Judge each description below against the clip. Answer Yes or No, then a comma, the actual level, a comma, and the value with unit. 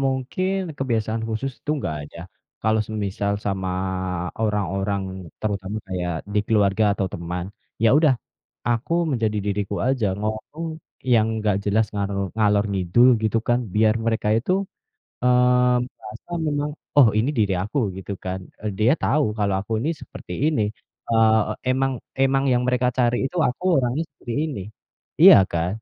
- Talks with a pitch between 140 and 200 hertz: No, low, 110 Hz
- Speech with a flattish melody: No, average, 3.8 semitones